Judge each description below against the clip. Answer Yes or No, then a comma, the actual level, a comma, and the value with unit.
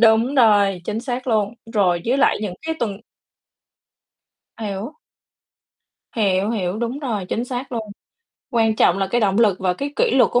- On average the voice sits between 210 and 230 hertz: Yes, high, 220 Hz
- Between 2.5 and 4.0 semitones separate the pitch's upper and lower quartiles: Yes, average, 3.6 semitones